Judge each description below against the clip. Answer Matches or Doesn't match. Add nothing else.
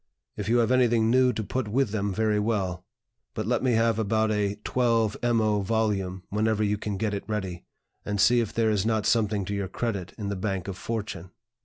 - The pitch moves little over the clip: Matches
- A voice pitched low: Matches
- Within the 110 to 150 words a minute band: Doesn't match